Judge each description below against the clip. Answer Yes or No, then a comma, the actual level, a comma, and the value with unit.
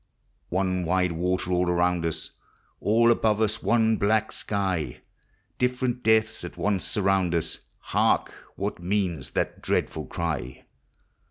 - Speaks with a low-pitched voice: Yes, very low, 95 Hz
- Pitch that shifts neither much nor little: Yes, average, 3.9 semitones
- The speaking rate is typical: No, slow, 125 wpm